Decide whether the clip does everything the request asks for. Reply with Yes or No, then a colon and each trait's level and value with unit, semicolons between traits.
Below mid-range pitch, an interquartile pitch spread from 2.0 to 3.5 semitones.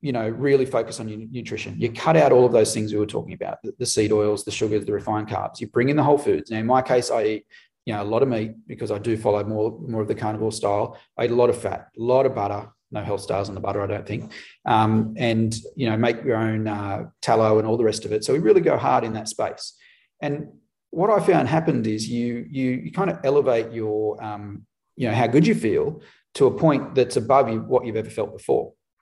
Yes: low, 110 Hz; average, 2.9 semitones